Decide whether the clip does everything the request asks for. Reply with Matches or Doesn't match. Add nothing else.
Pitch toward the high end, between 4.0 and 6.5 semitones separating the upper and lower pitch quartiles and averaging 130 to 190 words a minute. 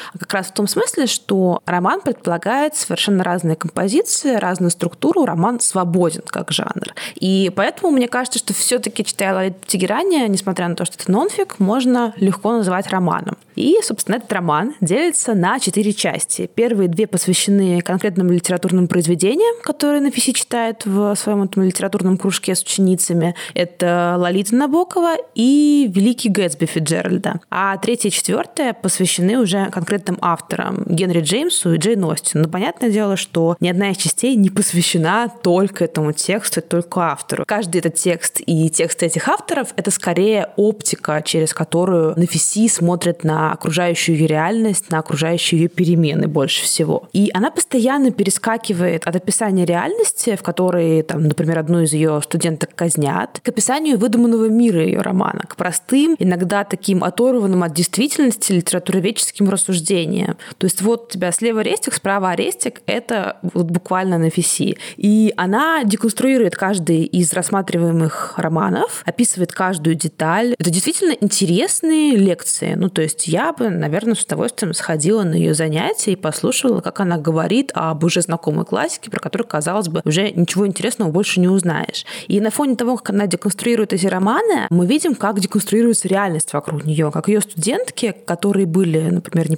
Matches